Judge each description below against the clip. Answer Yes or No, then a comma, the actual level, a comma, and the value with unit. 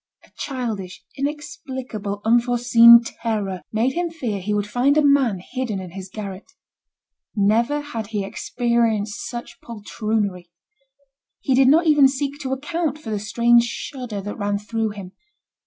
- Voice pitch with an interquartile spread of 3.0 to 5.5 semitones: Yes, average, 4.4 semitones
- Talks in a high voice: Yes, high, 235 Hz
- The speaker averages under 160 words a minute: Yes, average, 145 wpm